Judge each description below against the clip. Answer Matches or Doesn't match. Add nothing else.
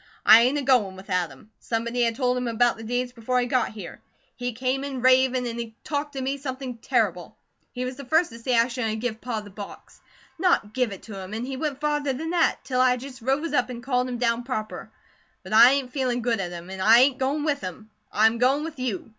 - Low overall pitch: Doesn't match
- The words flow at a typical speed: Doesn't match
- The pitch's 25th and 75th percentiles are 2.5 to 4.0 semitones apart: Matches